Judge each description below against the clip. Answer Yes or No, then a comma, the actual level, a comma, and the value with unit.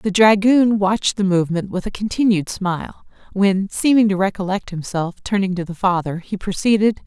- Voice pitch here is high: Yes, high, 195 Hz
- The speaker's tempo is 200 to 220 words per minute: No, average, 170 wpm